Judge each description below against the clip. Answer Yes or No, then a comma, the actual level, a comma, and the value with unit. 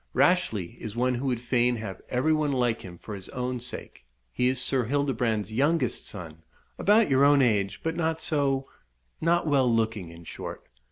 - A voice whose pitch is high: No, low, 125 Hz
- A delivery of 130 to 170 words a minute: No, average, 180 wpm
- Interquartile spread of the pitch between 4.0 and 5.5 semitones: Yes, average, 4.4 semitones